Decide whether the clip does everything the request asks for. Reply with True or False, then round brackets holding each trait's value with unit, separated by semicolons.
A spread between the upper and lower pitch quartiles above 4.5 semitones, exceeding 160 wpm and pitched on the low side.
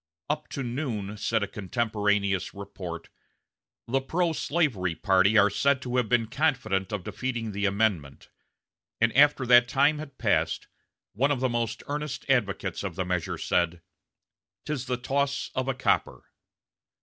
False (5.3 semitones; 150 wpm; 115 Hz)